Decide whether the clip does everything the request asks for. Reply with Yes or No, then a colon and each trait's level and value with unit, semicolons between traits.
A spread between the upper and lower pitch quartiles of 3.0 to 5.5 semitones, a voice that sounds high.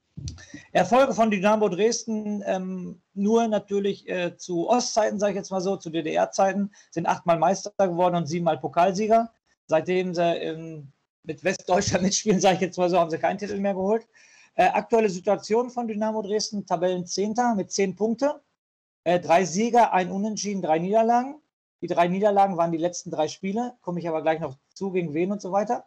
Yes: average, 3.7 semitones; high, 195 Hz